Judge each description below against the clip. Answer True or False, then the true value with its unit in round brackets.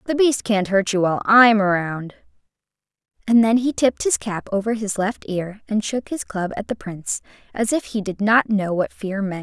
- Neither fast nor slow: False (215 wpm)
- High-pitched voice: True (210 Hz)